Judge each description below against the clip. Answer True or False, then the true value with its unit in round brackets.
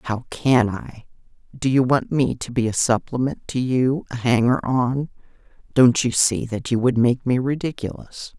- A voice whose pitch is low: True (125 Hz)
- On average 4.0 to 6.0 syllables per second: True (4.4 syllables/s)